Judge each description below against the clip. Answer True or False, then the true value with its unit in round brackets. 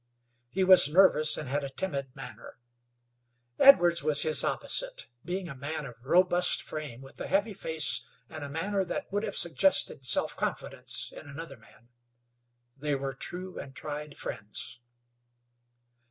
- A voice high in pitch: False (155 Hz)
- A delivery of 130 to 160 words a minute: True (150 wpm)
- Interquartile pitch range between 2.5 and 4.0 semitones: False (4.9 semitones)